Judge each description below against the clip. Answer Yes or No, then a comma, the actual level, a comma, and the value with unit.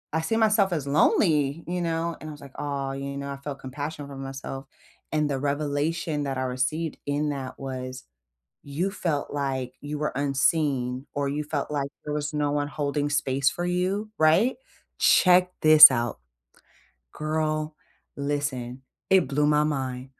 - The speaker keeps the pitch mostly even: Yes, narrow, 2.2 semitones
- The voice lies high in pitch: No, medium, 145 Hz